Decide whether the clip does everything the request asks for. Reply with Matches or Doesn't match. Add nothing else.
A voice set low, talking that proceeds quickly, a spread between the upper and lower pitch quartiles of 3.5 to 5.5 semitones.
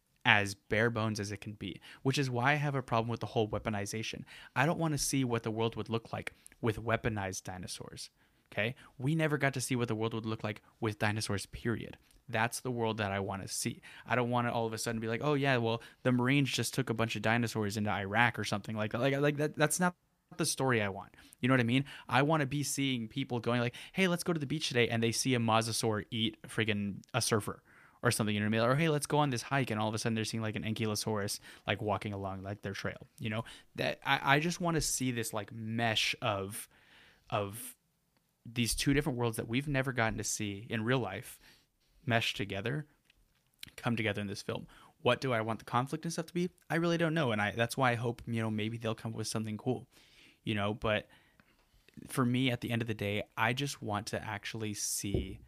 Matches